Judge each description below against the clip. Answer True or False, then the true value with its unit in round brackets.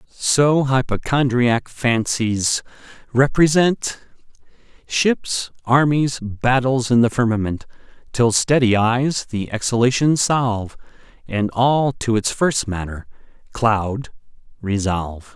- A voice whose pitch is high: False (120 Hz)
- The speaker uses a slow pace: True (95 wpm)